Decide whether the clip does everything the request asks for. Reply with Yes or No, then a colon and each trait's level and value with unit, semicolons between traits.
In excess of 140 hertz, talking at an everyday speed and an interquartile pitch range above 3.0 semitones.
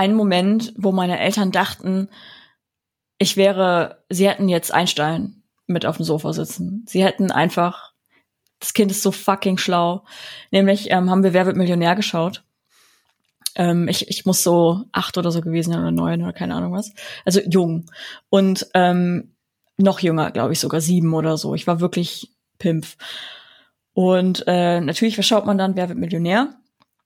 No: medium, 185 Hz; average, 170 wpm; narrow, 2.4 semitones